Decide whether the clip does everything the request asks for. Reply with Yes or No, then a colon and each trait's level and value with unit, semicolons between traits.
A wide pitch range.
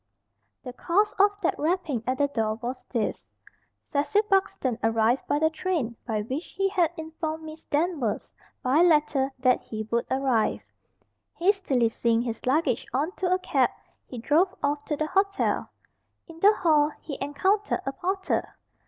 Yes: wide, 6.1 semitones